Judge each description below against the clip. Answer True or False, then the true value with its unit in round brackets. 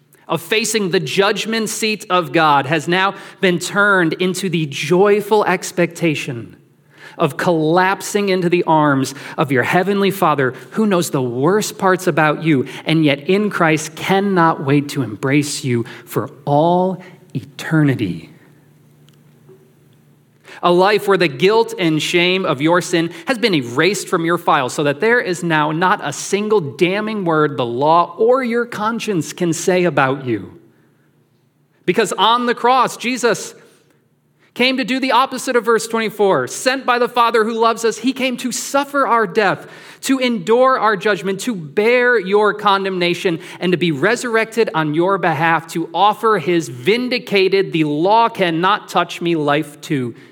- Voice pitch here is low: False (180 Hz)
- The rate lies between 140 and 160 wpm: True (155 wpm)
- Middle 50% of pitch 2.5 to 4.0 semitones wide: False (5.3 semitones)